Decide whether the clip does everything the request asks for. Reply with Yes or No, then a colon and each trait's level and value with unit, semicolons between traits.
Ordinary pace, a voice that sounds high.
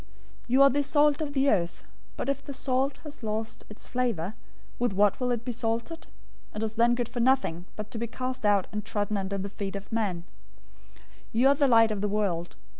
No: fast, 225 wpm; high, 230 Hz